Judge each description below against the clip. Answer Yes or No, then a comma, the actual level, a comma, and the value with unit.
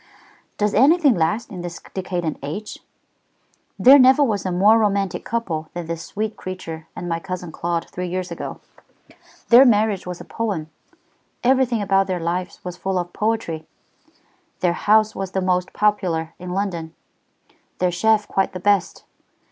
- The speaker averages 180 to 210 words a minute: No, average, 155 wpm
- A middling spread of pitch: Yes, average, 3.5 semitones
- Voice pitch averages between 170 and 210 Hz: Yes, medium, 185 Hz